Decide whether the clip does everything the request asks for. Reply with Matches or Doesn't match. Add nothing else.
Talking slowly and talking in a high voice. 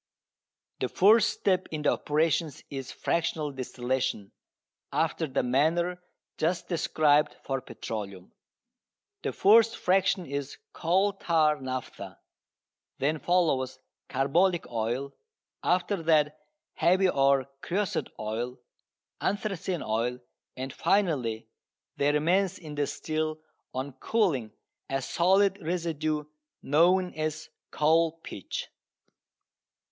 Doesn't match